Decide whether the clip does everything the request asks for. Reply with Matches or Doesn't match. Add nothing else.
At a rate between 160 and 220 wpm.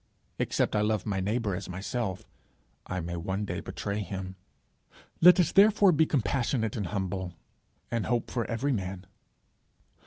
Doesn't match